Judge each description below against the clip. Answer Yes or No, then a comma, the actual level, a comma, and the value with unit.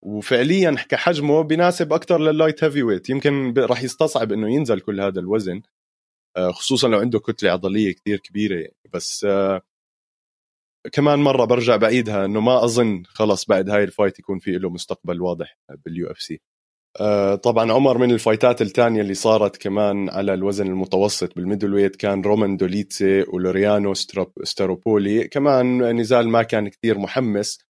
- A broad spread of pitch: No, average, 4.0 semitones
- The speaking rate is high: Yes, fast, 150 wpm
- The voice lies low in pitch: Yes, low, 105 Hz